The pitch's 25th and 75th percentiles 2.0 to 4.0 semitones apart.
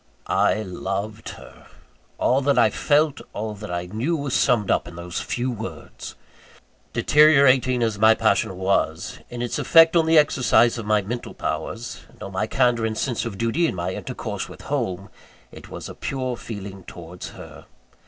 No: average, 4.8 semitones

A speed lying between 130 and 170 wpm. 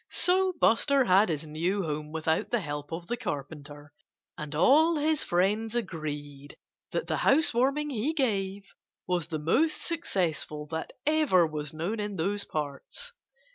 Yes: average, 150 wpm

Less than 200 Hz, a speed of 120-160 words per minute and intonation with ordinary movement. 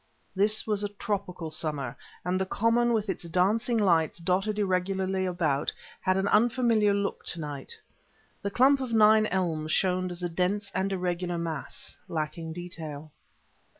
Yes: medium, 185 Hz; average, 155 wpm; average, 3.6 semitones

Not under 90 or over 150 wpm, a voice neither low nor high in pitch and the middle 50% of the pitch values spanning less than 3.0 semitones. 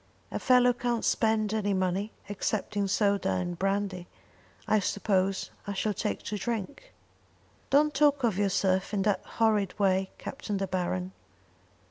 No: average, 145 wpm; high, 205 Hz; narrow, 2.6 semitones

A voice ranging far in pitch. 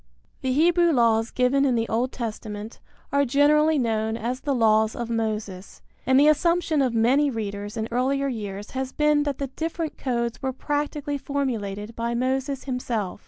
No: average, 4.0 semitones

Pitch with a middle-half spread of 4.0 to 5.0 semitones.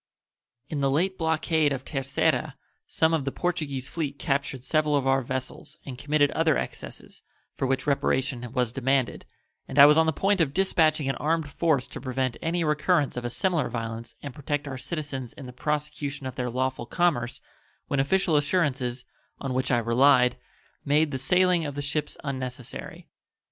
No: average, 3.0 semitones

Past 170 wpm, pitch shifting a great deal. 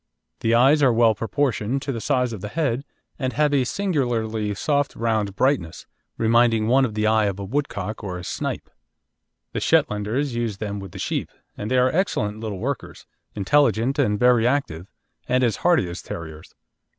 No: average, 180 wpm; average, 4.4 semitones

